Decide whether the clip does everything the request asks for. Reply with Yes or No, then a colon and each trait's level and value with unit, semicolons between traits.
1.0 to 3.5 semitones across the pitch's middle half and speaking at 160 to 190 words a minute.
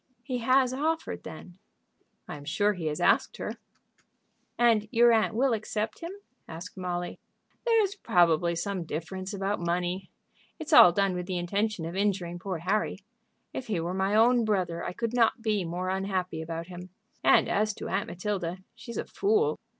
No: average, 4.4 semitones; average, 175 wpm